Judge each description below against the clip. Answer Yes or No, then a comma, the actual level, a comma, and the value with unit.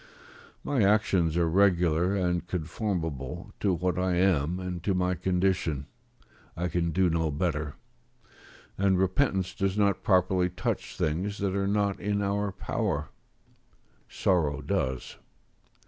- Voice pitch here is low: Yes, very low, 90 Hz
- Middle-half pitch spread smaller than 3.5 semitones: Yes, average, 2.8 semitones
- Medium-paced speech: No, slow, 130 wpm